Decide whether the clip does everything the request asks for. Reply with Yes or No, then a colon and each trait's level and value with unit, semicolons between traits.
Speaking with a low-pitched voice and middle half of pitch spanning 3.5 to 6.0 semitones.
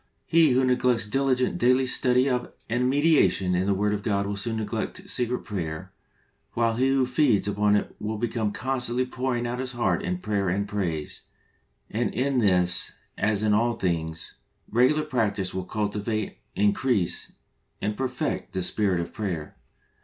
Yes: low, 110 Hz; average, 4.0 semitones